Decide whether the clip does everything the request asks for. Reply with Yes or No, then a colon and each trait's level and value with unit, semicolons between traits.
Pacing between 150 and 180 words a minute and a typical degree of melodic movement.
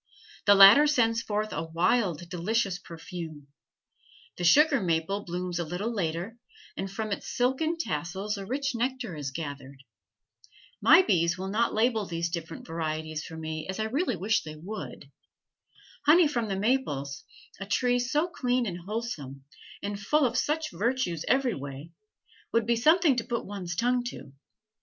No: average, 160 wpm; wide, 6.5 semitones